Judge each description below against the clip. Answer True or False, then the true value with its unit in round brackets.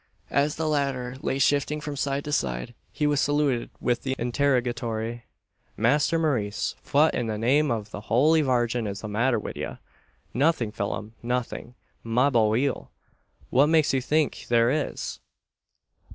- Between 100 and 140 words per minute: False (150 wpm)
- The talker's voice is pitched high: False (125 Hz)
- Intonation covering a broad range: False (3.9 semitones)